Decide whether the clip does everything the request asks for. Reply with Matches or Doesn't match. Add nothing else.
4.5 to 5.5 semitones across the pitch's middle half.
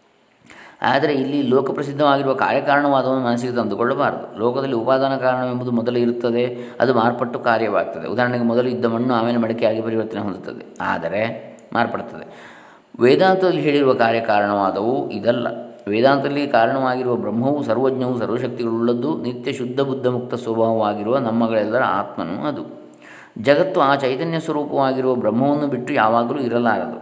Doesn't match